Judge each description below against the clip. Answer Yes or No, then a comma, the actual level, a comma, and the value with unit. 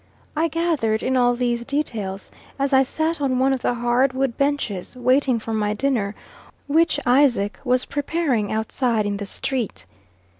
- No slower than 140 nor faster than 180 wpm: Yes, average, 160 wpm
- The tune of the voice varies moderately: Yes, average, 4.0 semitones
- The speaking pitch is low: No, very high, 255 Hz